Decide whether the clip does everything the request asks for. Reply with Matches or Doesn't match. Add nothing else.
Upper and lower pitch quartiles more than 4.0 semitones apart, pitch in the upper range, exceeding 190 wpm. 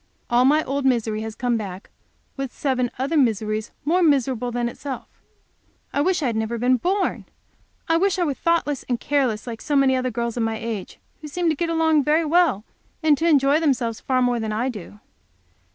Matches